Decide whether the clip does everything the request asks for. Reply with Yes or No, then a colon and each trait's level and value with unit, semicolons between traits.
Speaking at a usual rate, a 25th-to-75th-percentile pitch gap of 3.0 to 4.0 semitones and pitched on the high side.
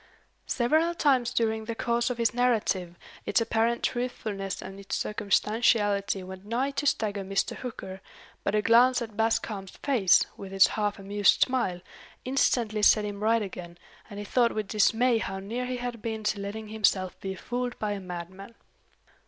Yes: average, 170 wpm; average, 3.3 semitones; high, 215 Hz